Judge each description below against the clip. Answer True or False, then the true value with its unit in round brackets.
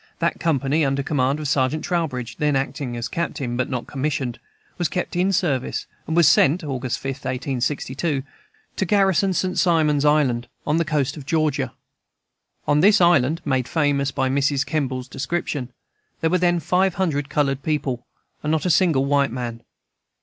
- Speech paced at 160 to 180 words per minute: True (165 wpm)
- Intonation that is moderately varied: True (3.8 semitones)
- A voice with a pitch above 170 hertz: False (145 Hz)